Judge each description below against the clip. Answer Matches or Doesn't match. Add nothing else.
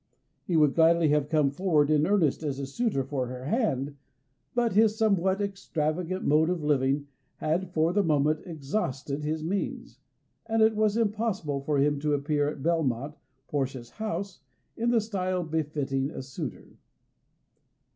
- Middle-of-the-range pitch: Matches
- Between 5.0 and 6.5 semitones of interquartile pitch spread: Matches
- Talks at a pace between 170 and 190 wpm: Doesn't match